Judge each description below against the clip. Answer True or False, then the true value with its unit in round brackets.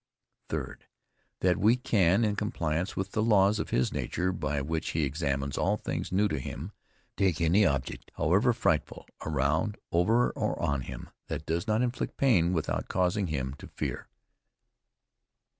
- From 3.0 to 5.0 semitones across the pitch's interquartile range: False (5.4 semitones)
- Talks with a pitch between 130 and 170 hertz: False (90 Hz)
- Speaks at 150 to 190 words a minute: True (160 wpm)